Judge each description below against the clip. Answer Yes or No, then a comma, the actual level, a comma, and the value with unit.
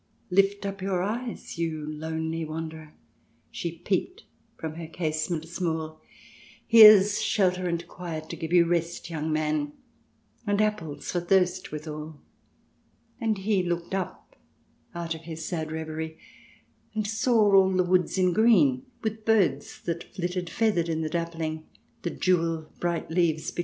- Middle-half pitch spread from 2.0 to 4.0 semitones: Yes, average, 3.2 semitones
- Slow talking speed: No, average, 155 wpm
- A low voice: No, medium, 170 Hz